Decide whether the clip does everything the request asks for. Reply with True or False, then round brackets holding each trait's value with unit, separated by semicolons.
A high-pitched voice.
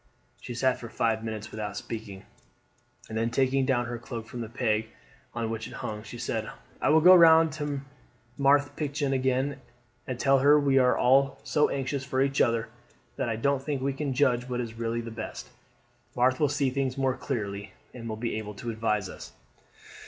False (125 Hz)